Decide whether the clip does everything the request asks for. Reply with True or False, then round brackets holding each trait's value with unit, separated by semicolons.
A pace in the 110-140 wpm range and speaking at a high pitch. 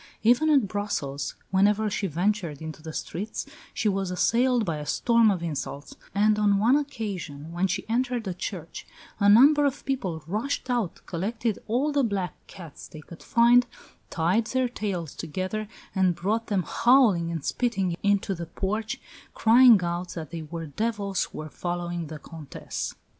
False (165 wpm; 200 Hz)